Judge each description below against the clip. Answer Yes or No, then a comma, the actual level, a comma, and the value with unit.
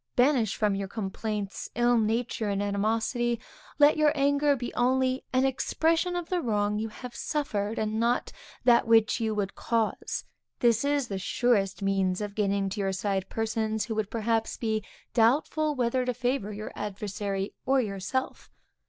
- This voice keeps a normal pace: Yes, average, 165 wpm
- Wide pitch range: No, average, 3.6 semitones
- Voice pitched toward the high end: Yes, high, 225 Hz